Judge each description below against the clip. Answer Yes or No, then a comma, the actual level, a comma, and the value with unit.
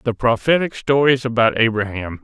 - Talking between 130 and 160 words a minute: Yes, slow, 135 wpm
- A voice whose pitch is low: Yes, low, 120 Hz